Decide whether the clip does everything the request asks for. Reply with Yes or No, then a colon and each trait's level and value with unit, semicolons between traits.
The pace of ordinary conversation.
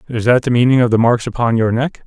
No: fast, 290 wpm